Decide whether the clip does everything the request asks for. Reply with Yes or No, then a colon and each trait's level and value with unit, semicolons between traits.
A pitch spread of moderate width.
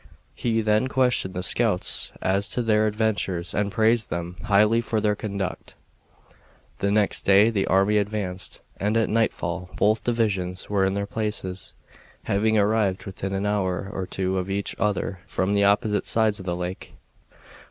No: narrow, 2.3 semitones